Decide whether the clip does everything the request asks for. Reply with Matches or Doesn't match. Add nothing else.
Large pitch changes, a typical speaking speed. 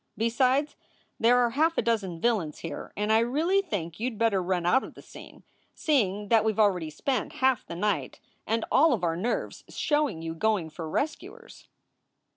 Matches